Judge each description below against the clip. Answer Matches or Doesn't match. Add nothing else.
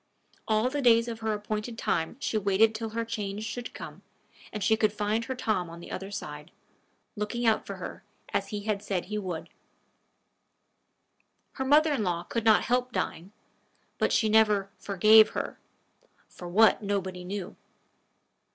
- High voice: Matches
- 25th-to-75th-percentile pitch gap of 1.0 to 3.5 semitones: Matches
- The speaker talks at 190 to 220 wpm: Doesn't match